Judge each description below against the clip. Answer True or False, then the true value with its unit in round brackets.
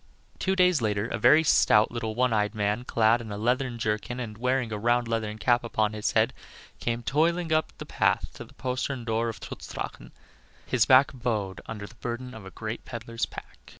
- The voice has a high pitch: False (115 Hz)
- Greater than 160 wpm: True (205 wpm)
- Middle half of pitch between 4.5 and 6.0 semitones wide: False (2.7 semitones)